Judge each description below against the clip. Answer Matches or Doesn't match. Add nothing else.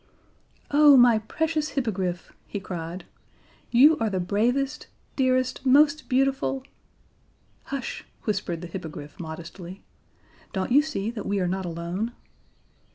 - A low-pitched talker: Doesn't match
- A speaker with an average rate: Doesn't match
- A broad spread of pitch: Matches